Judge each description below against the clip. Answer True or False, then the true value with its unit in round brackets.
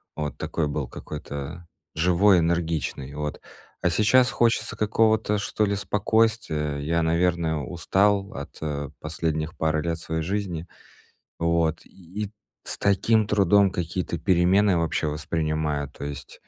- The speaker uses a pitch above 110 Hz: False (85 Hz)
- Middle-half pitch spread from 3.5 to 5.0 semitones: True (4.5 semitones)